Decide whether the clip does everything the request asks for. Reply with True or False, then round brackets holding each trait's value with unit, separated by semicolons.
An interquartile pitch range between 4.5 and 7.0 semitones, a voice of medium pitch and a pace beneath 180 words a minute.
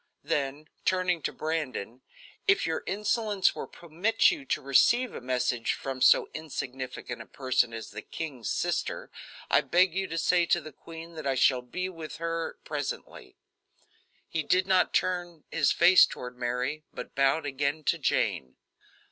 True (5.4 semitones; 155 Hz; 160 wpm)